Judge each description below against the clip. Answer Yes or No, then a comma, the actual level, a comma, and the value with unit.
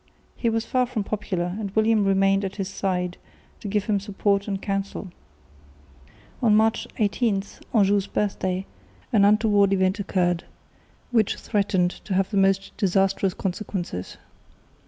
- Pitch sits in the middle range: No, high, 195 Hz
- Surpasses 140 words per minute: No, slow, 135 wpm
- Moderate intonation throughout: No, narrow, 1.7 semitones